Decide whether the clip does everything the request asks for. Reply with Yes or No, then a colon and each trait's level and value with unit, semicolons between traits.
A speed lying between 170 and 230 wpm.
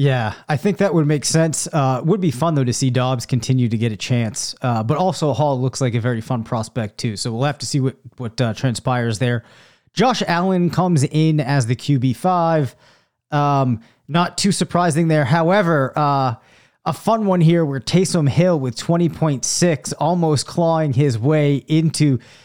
Yes: average, 190 wpm